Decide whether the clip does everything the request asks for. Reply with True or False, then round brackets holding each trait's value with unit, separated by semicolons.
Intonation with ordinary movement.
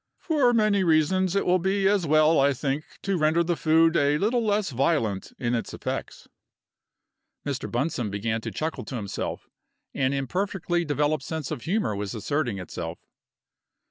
False (6.3 semitones)